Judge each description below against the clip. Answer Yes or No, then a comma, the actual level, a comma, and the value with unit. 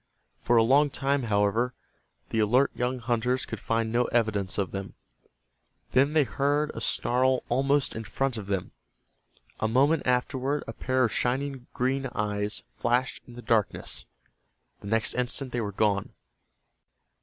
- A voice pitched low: Yes, low, 125 Hz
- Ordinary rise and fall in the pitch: Yes, average, 3.4 semitones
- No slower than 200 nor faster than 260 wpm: No, average, 155 wpm